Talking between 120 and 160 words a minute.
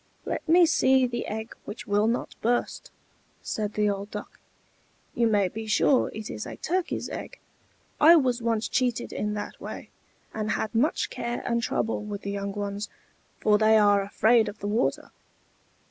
No: average, 175 wpm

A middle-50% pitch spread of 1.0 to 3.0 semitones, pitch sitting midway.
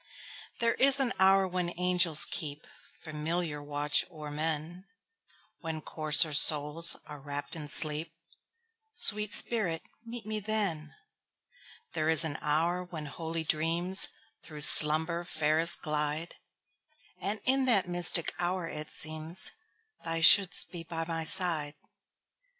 No: average, 3.6 semitones; medium, 165 Hz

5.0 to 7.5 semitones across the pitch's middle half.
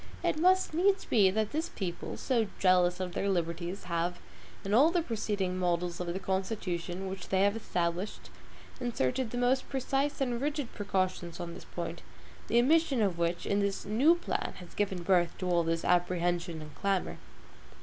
Yes: wide, 5.4 semitones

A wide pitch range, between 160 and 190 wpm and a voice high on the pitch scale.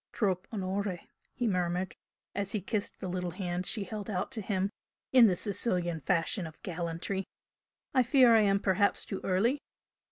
No: average, 2.8 semitones; average, 165 wpm; high, 195 Hz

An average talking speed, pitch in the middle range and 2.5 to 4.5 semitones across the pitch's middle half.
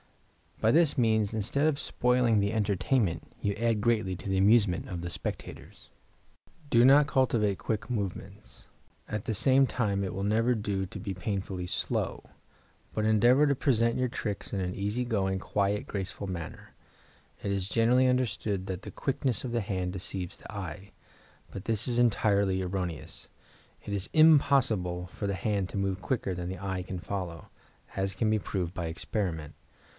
No: average, 170 wpm; low, 100 Hz; average, 3.8 semitones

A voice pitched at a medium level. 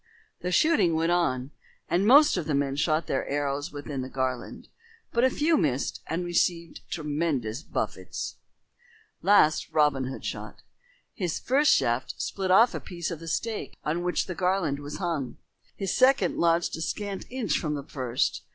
Yes: medium, 165 Hz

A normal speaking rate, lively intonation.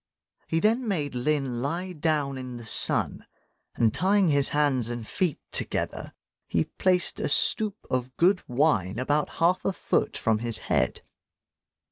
Yes: average, 150 wpm; wide, 6.4 semitones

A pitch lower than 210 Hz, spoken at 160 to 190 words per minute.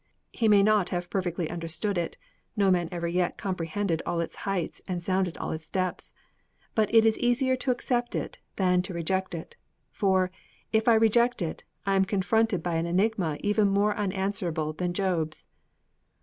Yes: high, 190 Hz; average, 175 wpm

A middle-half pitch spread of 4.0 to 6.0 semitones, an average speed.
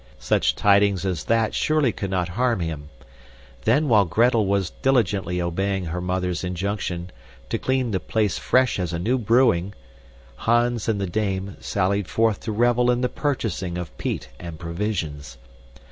Yes: average, 4.5 semitones; average, 160 wpm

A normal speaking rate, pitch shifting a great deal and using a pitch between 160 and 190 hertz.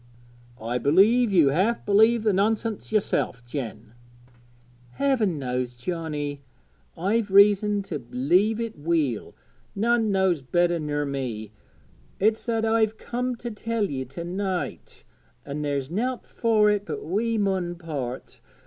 No: slow, 130 wpm; wide, 7.3 semitones; medium, 185 Hz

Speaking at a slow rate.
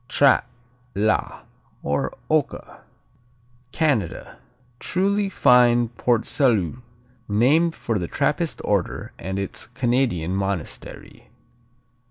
Yes: slow, 90 wpm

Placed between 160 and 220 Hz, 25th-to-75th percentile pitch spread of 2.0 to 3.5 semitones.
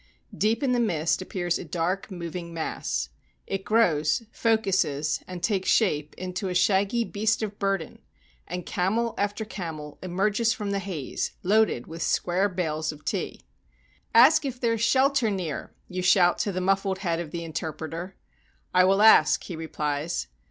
No: medium, 185 Hz; average, 4.2 semitones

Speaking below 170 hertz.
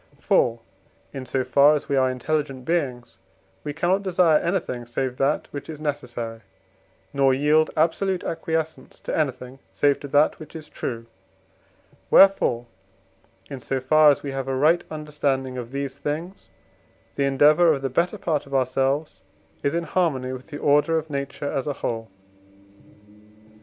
Yes: medium, 140 Hz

